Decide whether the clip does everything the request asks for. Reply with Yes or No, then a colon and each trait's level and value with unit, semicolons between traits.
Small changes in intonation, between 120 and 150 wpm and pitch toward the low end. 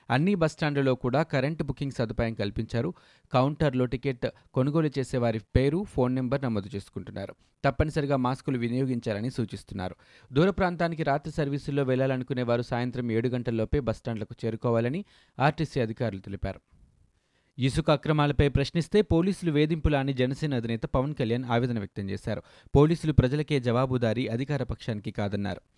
No: average, 3.9 semitones; fast, 125 wpm; low, 130 Hz